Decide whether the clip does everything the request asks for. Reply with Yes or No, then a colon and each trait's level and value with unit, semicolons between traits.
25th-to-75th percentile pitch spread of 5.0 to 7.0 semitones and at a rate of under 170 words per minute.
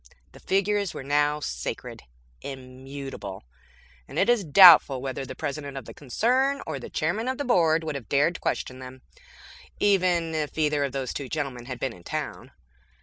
No: average, 5.3 semitones; average, 175 wpm